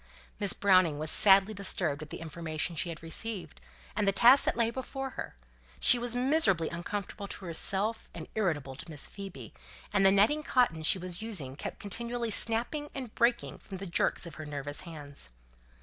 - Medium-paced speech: Yes, average, 180 wpm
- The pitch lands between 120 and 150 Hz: No, high, 195 Hz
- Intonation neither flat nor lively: No, wide, 6.0 semitones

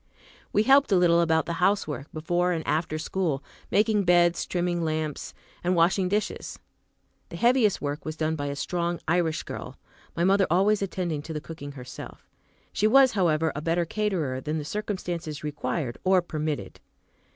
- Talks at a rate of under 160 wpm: No, average, 165 wpm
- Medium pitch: Yes, medium, 170 Hz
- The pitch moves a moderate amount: Yes, average, 3.4 semitones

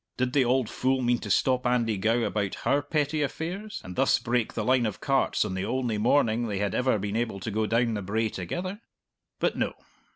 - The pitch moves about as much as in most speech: Yes, average, 3.6 semitones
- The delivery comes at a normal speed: No, fast, 220 wpm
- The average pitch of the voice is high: No, low, 120 Hz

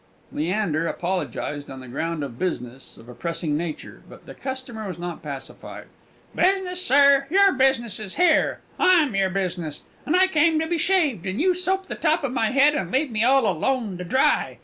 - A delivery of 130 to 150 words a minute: No, average, 195 wpm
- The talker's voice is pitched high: Yes, high, 230 Hz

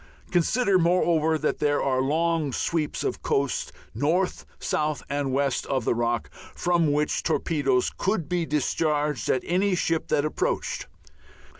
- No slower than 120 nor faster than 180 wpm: Yes, average, 140 wpm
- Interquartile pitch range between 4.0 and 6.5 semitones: No, average, 3.3 semitones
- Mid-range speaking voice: Yes, medium, 150 Hz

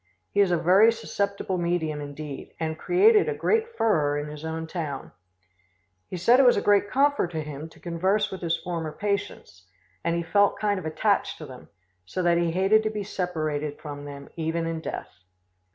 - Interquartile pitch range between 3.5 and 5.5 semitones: Yes, average, 4.5 semitones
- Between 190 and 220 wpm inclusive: Yes, average, 195 wpm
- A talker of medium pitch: Yes, medium, 170 Hz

